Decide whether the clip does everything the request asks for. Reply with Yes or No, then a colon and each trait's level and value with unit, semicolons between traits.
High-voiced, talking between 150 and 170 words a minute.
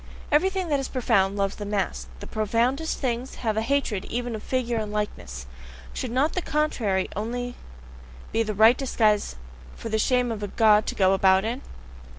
No: high, 225 Hz; average, 180 wpm